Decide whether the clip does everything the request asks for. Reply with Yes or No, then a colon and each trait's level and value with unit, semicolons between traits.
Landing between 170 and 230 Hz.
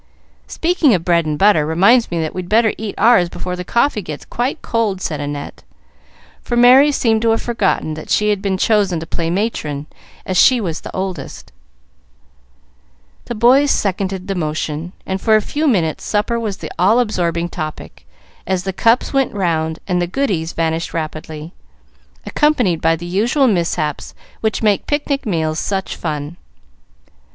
Yes: high, 190 Hz